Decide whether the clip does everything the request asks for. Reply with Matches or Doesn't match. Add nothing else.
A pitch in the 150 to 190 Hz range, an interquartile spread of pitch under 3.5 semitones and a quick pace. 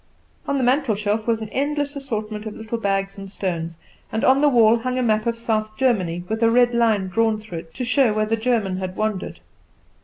Doesn't match